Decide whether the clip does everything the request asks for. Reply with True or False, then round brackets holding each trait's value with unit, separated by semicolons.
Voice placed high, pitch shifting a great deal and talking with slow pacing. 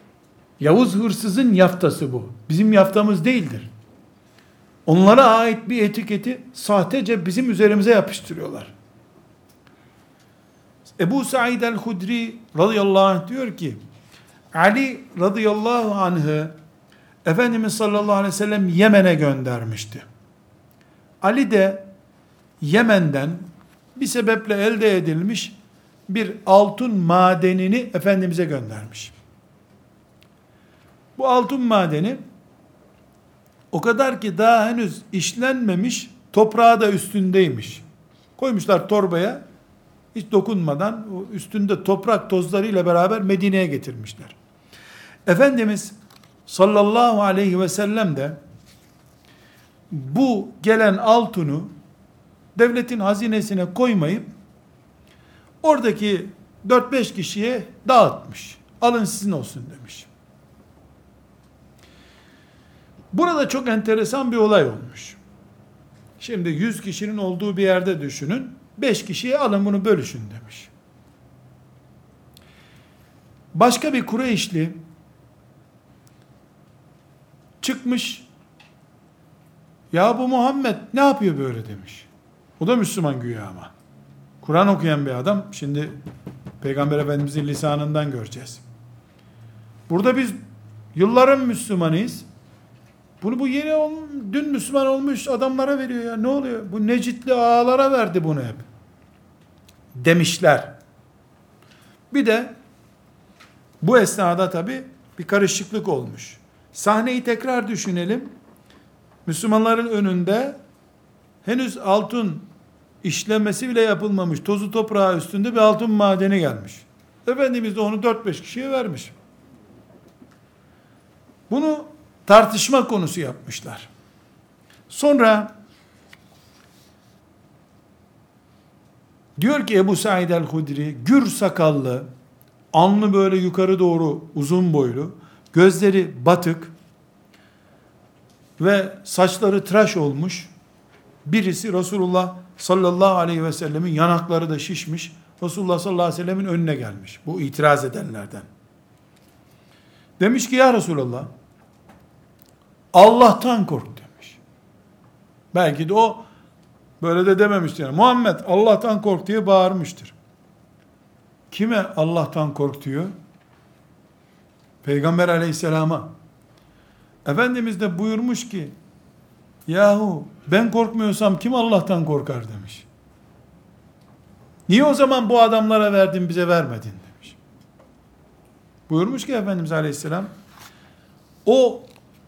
True (195 Hz; 5.9 semitones; 90 wpm)